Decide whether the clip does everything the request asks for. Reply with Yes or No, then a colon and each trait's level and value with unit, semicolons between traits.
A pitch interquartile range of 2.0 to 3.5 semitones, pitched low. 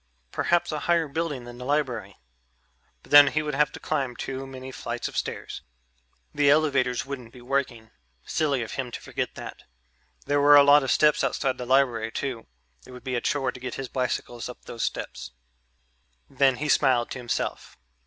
Yes: average, 2.8 semitones; low, 130 Hz